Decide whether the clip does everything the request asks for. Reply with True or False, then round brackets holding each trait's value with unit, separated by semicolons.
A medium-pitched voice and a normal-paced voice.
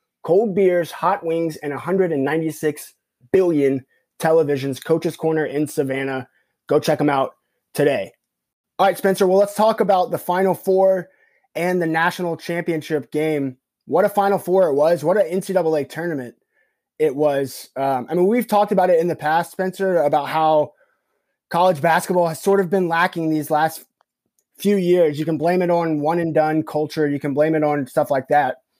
True (160 Hz; 175 wpm)